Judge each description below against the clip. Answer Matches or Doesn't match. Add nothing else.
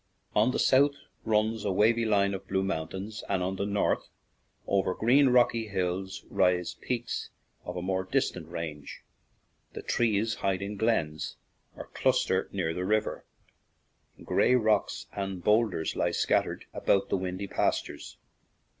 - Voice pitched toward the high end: Doesn't match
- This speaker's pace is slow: Doesn't match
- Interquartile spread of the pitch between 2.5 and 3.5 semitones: Matches